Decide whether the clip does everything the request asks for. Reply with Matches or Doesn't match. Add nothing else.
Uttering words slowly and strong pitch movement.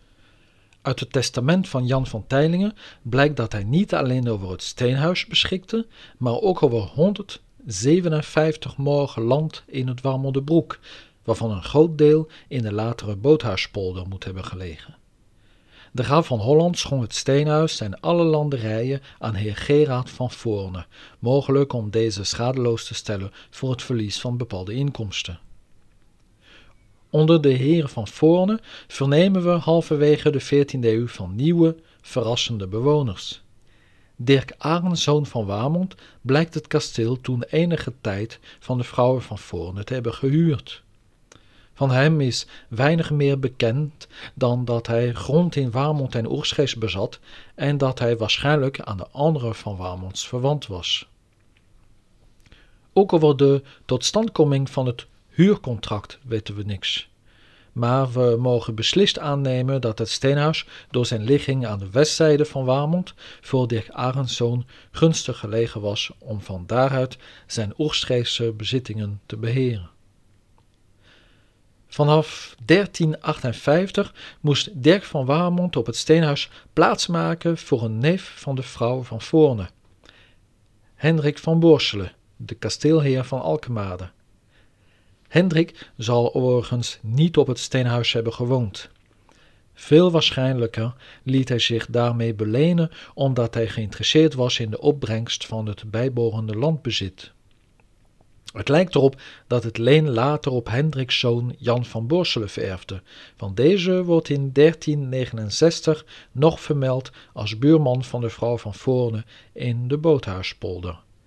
Doesn't match